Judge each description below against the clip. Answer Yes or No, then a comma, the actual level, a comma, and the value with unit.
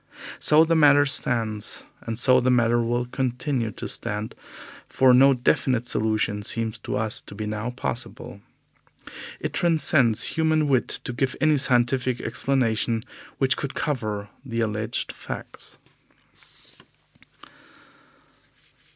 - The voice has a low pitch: Yes, low, 125 Hz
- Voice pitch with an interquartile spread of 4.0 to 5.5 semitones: No, average, 3.4 semitones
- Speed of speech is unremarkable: No, slow, 120 wpm